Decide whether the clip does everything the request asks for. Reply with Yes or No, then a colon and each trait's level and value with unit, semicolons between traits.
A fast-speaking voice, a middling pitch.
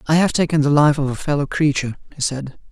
Yes: fast, 245 wpm; medium, 145 Hz